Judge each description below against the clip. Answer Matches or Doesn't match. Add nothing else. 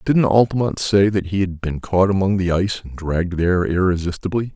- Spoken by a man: Matches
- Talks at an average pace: Doesn't match